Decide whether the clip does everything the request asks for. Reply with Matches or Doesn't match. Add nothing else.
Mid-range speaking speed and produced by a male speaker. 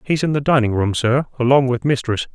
Doesn't match